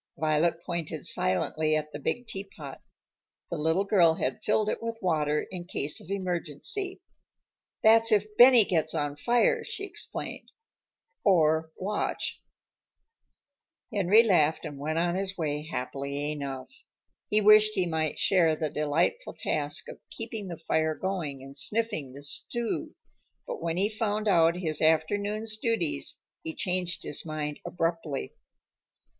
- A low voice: No, medium, 170 Hz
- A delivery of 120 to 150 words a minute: Yes, average, 140 wpm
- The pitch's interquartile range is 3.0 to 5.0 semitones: No, wide, 5.5 semitones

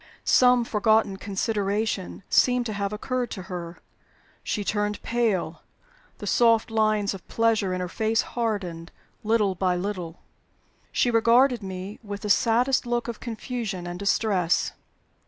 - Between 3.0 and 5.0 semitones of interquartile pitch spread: Yes, average, 3.3 semitones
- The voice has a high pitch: Yes, high, 210 Hz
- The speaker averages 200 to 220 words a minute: No, slow, 135 wpm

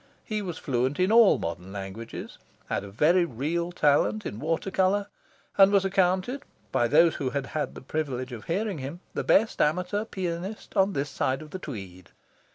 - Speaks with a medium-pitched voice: Yes, medium, 165 Hz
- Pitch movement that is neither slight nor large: No, wide, 6.6 semitones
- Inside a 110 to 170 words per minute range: No, average, 180 wpm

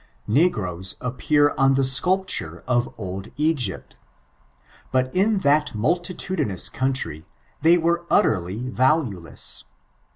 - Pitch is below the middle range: Yes, low, 130 Hz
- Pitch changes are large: Yes, wide, 8.1 semitones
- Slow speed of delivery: Yes, slow, 100 wpm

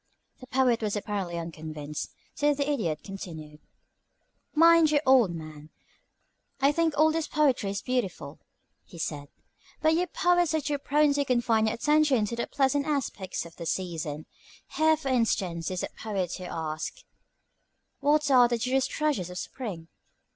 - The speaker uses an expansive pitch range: Yes, wide, 9.0 semitones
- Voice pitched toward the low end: No, high, 235 Hz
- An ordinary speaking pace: Yes, average, 160 wpm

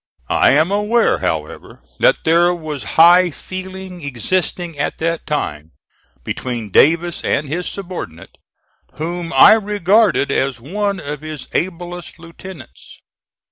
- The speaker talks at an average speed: No, slow, 120 wpm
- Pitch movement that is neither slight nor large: Yes, average, 4.1 semitones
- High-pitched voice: No, medium, 170 Hz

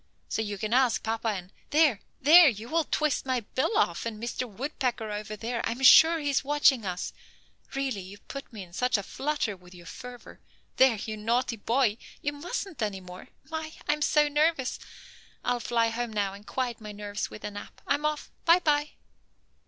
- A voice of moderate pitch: No, high, 240 Hz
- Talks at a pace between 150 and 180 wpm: No, average, 195 wpm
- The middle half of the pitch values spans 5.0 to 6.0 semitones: Yes, wide, 5.6 semitones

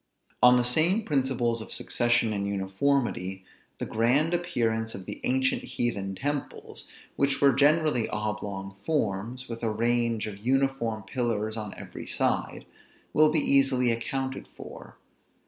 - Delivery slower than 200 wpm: Yes, slow, 135 wpm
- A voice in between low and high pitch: No, low, 120 Hz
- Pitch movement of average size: Yes, average, 4.0 semitones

